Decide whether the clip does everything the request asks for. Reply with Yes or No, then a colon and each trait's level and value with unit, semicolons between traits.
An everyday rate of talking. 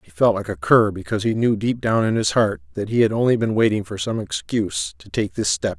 No: fast, 270 wpm